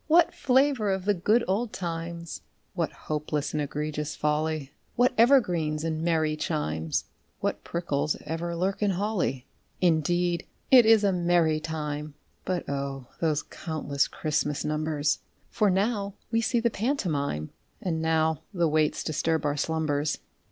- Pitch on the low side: No, medium, 160 Hz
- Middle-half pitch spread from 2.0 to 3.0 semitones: No, average, 4.2 semitones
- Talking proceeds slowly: No, average, 145 wpm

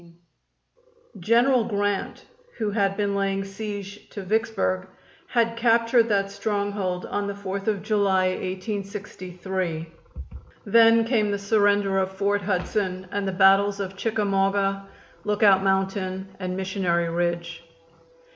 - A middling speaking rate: No, slow, 120 wpm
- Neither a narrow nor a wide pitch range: No, narrow, 1.6 semitones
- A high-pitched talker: Yes, high, 200 Hz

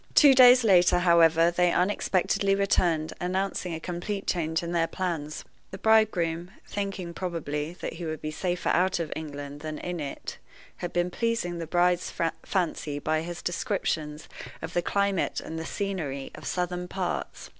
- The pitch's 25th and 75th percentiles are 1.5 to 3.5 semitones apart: Yes, average, 2.7 semitones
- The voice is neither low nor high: Yes, medium, 175 Hz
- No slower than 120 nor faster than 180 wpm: Yes, average, 160 wpm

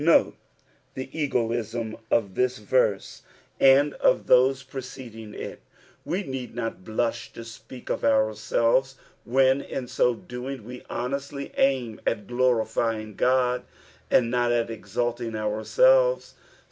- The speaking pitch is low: Yes, low, 120 Hz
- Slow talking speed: Yes, slow, 120 wpm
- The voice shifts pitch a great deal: No, average, 2.8 semitones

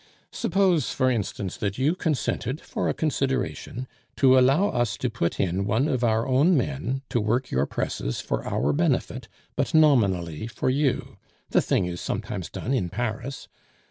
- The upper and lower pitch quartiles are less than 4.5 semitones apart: No, average, 5.3 semitones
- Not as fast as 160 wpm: No, average, 165 wpm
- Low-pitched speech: Yes, low, 125 Hz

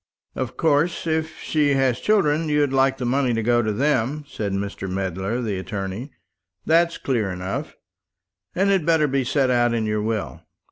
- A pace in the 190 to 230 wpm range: No, average, 175 wpm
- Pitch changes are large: Yes, wide, 5.8 semitones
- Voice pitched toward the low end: Yes, low, 130 Hz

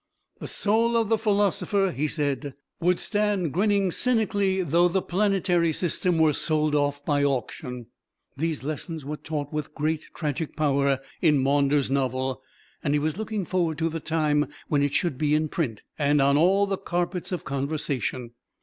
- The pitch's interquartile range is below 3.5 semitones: No, average, 4.4 semitones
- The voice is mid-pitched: Yes, medium, 155 Hz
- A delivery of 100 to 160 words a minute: No, average, 170 wpm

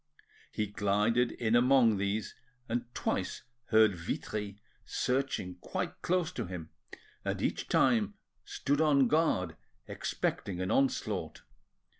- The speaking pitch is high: No, low, 110 Hz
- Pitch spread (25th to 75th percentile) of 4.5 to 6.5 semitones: Yes, wide, 5.5 semitones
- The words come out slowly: Yes, slow, 115 wpm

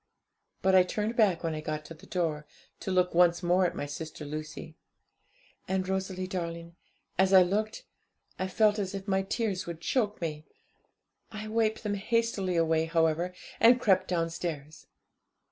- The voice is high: No, medium, 180 Hz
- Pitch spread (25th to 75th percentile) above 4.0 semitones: No, average, 3.3 semitones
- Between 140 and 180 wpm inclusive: Yes, average, 160 wpm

